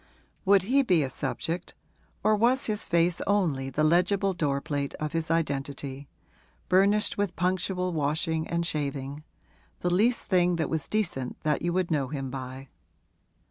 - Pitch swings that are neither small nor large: Yes, average, 4.7 semitones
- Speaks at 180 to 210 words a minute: No, average, 155 wpm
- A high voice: No, medium, 165 Hz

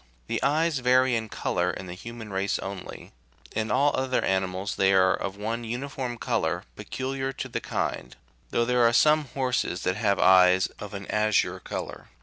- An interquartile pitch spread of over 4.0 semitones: Yes, average, 5.1 semitones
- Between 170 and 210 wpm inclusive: Yes, average, 175 wpm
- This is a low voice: Yes, low, 110 Hz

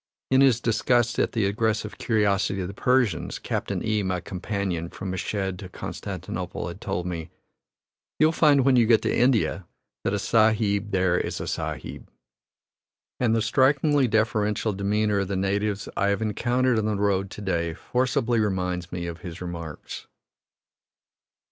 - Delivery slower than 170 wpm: Yes, average, 160 wpm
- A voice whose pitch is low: Yes, low, 105 Hz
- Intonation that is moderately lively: Yes, average, 3.4 semitones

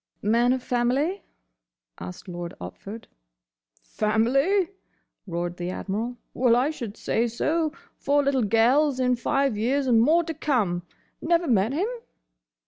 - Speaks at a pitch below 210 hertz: No, high, 245 Hz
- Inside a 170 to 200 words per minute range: No, slow, 135 wpm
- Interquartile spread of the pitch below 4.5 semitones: No, average, 5.1 semitones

